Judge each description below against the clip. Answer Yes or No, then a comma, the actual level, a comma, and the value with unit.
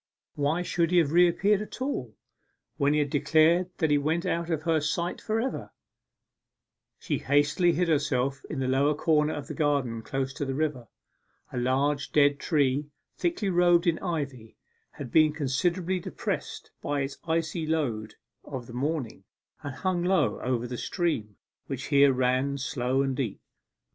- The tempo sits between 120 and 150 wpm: No, average, 165 wpm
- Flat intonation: No, average, 4.1 semitones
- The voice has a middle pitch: Yes, medium, 145 Hz